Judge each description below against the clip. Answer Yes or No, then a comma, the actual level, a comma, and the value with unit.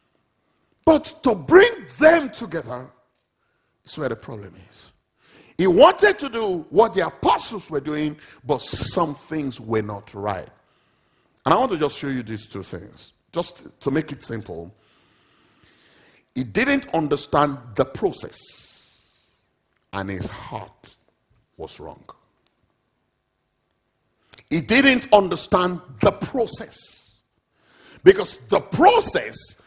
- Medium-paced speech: No, slow, 115 wpm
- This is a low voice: No, medium, 150 Hz